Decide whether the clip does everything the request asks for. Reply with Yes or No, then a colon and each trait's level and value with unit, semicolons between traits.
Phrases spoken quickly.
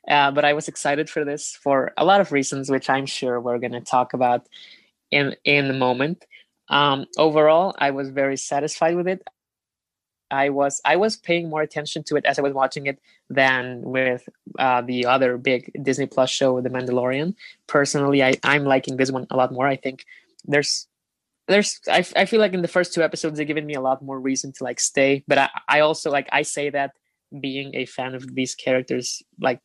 Yes: fast, 215 wpm